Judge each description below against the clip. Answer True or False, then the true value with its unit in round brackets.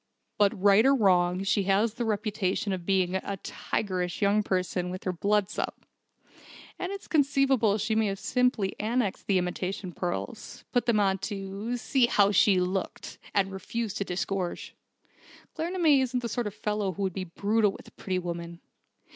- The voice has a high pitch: True (200 Hz)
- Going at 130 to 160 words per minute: False (170 wpm)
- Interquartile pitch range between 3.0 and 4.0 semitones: True (3.3 semitones)